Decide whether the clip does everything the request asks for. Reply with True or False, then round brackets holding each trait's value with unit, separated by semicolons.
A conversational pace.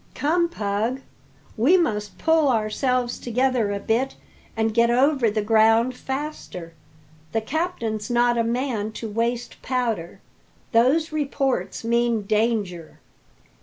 False (120 wpm)